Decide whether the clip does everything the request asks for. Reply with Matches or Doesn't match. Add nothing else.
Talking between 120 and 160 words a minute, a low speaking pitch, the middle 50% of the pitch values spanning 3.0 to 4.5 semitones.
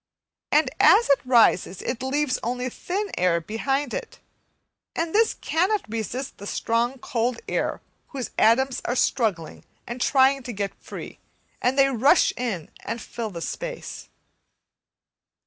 Doesn't match